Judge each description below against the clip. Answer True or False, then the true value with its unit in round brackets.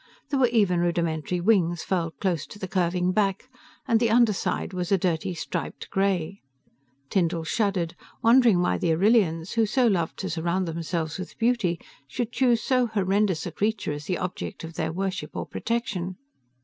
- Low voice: False (185 Hz)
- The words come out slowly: False (170 wpm)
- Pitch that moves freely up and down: False (4.3 semitones)